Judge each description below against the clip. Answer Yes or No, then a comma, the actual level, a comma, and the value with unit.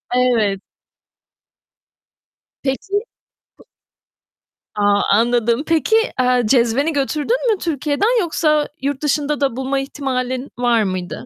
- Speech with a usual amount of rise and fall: Yes, average, 3.7 semitones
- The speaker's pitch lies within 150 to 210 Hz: No, very high, 270 Hz